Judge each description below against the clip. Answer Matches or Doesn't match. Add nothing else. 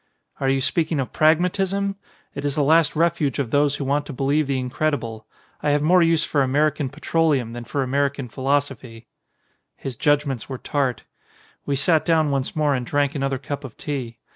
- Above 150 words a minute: Matches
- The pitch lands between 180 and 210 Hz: Doesn't match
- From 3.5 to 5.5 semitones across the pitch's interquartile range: Doesn't match